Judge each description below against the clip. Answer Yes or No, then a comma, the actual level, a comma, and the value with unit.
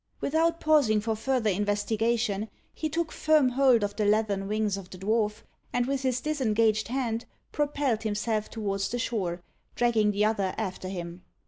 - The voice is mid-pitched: No, high, 220 Hz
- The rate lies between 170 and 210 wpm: No, average, 160 wpm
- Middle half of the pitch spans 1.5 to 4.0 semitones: Yes, average, 3.6 semitones